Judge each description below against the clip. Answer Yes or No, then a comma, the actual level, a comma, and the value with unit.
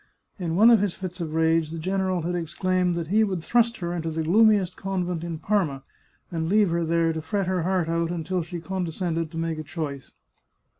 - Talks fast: Yes, fast, 210 wpm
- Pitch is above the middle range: No, medium, 170 Hz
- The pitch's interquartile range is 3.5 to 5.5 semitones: No, narrow, 2.5 semitones